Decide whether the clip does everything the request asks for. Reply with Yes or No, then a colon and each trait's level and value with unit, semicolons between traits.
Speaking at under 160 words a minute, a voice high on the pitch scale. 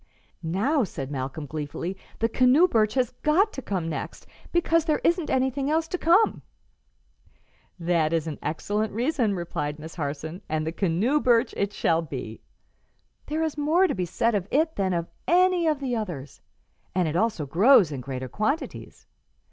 No: average, 170 wpm; high, 205 Hz